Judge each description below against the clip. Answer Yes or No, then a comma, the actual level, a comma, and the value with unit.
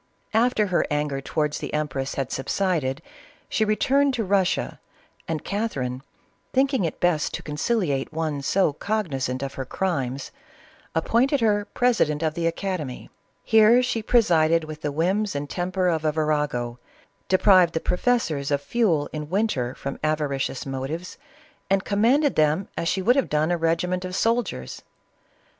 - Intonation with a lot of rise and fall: Yes, wide, 5.9 semitones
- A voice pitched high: No, medium, 165 Hz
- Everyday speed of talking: Yes, average, 150 wpm